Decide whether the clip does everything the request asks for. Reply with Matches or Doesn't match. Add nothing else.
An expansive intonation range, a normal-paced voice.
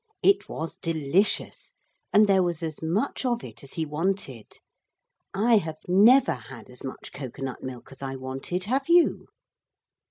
Matches